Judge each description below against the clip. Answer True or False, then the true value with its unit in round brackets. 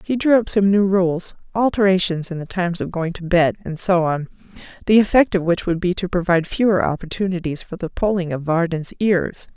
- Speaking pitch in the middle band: True (180 Hz)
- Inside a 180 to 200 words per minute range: True (195 wpm)